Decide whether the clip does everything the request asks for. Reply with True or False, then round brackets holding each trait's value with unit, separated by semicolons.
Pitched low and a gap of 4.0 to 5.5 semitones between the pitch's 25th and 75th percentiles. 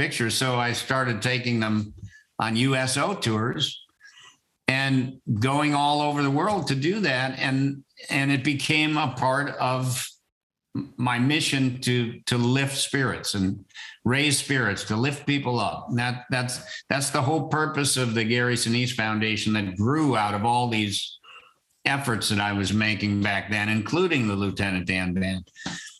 True (125 Hz; 4.3 semitones)